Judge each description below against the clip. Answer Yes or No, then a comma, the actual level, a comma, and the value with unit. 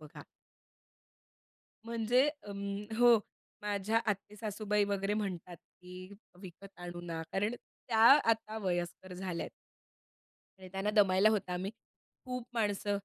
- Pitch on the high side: Yes, high, 200 Hz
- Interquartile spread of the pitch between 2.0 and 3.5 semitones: Yes, narrow, 2.6 semitones